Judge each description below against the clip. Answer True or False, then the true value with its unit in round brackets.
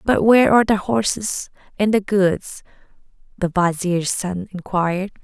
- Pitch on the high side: True (195 Hz)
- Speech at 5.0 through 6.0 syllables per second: False (4.5 syllables/s)